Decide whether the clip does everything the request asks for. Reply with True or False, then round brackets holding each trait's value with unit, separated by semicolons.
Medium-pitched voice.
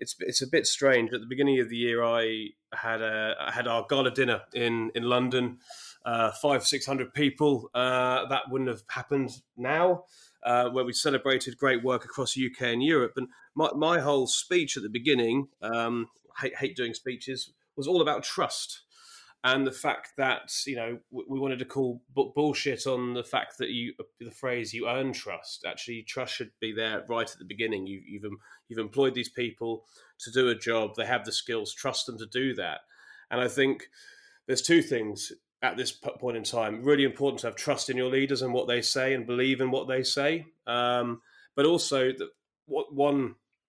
False (130 Hz)